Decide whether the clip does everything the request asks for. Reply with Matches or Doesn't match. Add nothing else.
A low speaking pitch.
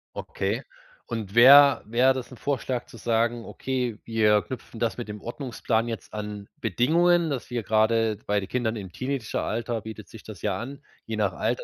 Matches